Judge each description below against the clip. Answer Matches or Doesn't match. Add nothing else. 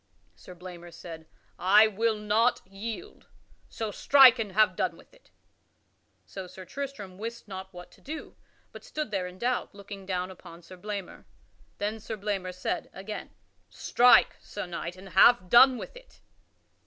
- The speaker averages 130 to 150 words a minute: Doesn't match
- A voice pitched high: Matches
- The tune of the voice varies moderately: Matches